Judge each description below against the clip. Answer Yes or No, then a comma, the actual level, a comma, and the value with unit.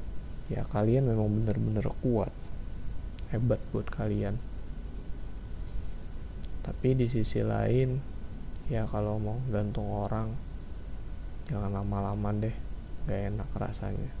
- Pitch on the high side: No, low, 105 Hz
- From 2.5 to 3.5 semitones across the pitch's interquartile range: Yes, average, 3.0 semitones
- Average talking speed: Yes, average, 95 wpm